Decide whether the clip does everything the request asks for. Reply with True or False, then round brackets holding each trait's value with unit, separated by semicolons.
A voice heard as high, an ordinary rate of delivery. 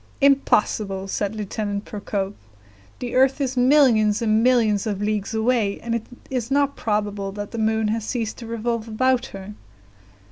True (220 Hz; 155 wpm)